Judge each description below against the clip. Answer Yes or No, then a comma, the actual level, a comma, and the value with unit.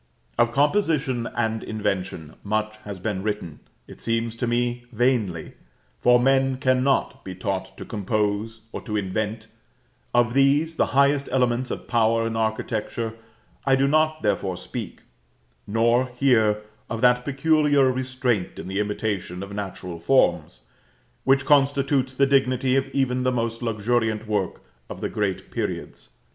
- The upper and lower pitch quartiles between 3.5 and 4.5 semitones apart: Yes, average, 4.0 semitones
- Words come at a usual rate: Yes, average, 145 wpm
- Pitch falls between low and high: No, low, 115 Hz